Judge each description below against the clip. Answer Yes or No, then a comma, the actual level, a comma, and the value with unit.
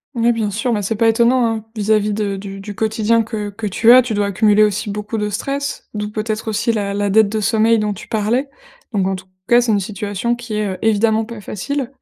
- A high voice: Yes, high, 215 Hz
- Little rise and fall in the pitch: Yes, narrow, 1.9 semitones